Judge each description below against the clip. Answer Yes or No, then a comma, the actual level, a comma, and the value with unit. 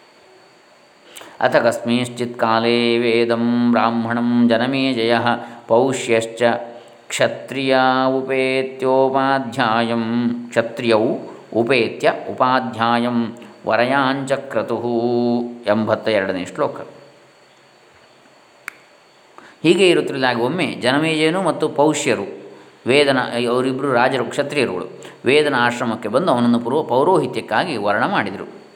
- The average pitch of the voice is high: No, low, 120 Hz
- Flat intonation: Yes, narrow, 2.0 semitones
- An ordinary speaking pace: Yes, average, 75 wpm